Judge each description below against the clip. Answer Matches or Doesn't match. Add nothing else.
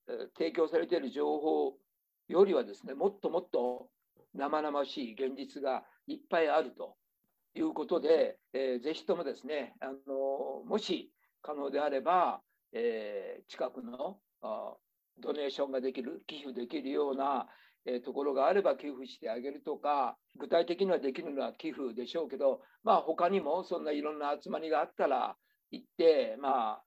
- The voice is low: Doesn't match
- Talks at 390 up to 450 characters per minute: Doesn't match